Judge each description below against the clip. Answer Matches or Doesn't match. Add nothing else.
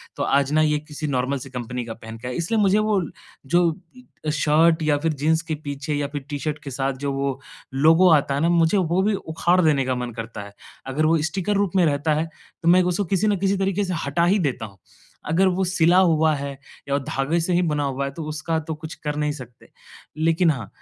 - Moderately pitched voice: Matches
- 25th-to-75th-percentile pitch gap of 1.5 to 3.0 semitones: Doesn't match